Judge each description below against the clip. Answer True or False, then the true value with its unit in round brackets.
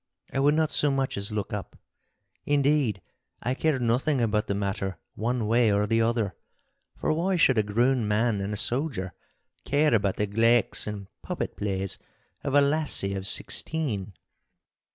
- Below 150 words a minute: False (165 wpm)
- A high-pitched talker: False (115 Hz)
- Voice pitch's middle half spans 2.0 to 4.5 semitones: False (5.1 semitones)